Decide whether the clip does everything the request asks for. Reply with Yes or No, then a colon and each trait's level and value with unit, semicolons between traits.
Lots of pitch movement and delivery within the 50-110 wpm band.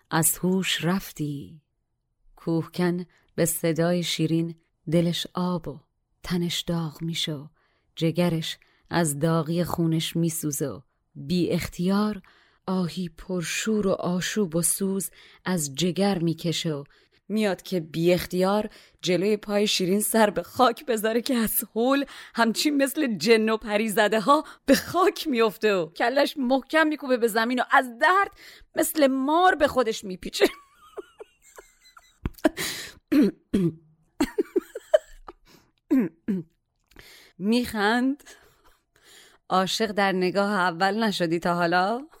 Yes: wide, 6.3 semitones; slow, 105 wpm